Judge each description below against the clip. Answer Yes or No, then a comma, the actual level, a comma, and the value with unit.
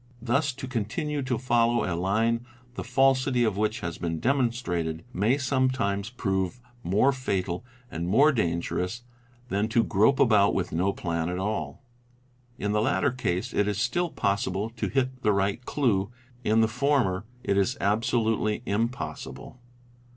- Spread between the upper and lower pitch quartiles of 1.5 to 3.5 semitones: No, average, 4.6 semitones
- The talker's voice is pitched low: Yes, low, 110 Hz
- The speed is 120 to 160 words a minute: Yes, average, 150 wpm